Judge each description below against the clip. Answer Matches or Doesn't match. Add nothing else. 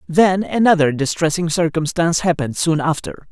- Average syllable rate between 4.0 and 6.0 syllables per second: Matches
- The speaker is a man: Matches